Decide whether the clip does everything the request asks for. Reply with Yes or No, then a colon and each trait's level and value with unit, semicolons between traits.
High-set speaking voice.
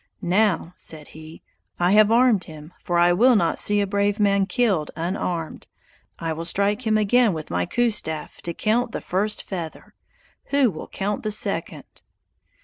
Yes: high, 200 Hz